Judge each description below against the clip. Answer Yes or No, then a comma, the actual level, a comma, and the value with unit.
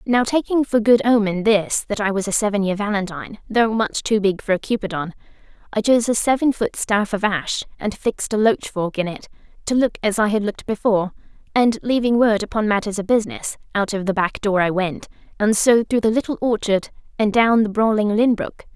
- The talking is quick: Yes, fast, 220 wpm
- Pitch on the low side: No, high, 215 Hz